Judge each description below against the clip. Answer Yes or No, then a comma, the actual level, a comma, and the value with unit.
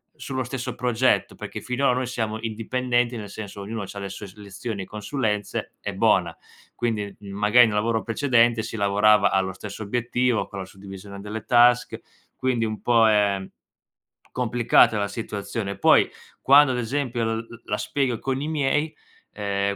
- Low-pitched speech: Yes, low, 110 Hz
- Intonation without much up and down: No, average, 3.3 semitones